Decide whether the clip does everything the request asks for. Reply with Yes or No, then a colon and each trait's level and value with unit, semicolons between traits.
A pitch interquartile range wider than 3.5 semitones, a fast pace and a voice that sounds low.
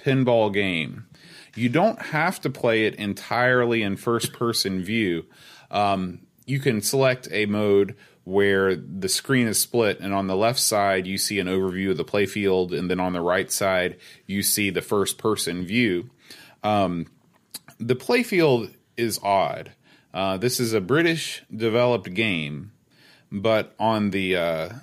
No: average, 4.1 semitones; average, 160 wpm; low, 105 Hz